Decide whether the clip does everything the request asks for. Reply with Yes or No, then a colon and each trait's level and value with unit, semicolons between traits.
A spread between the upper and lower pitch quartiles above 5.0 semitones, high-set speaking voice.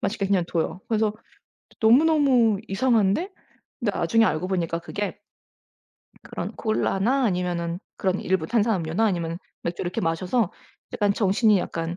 No: average, 4.3 semitones; high, 195 Hz